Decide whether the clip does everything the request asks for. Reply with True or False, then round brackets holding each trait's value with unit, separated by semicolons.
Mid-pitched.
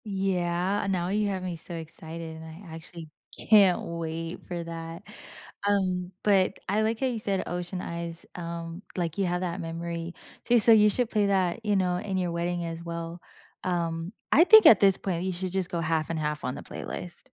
True (175 Hz)